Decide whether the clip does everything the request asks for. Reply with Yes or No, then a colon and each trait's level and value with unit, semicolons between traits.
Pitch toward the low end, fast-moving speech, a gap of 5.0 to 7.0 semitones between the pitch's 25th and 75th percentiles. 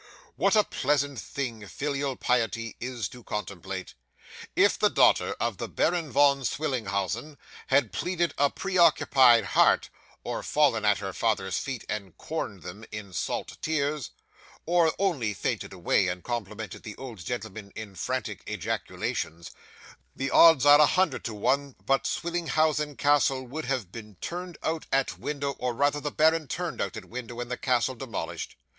No: low, 130 Hz; average, 155 wpm; wide, 5.6 semitones